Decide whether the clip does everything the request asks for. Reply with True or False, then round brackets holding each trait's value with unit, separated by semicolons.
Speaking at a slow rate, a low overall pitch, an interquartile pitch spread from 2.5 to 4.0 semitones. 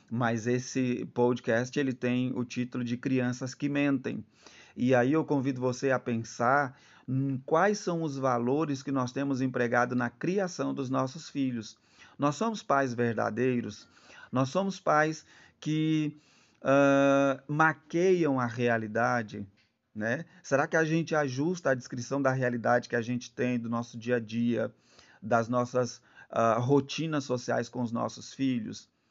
False (150 wpm; 130 Hz; 2.8 semitones)